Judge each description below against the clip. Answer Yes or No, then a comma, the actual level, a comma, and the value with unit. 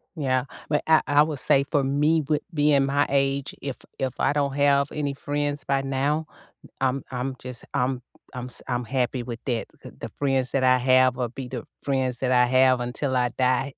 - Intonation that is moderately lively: No, narrow, 2.0 semitones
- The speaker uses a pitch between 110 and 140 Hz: Yes, low, 135 Hz